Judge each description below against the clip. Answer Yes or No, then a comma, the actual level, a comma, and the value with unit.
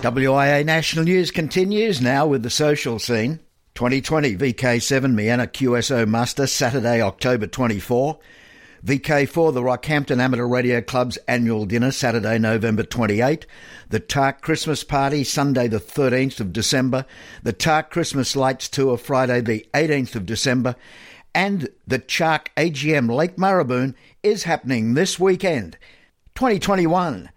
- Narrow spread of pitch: No, average, 4.1 semitones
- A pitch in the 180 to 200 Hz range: No, low, 130 Hz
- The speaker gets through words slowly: Yes, slow, 125 wpm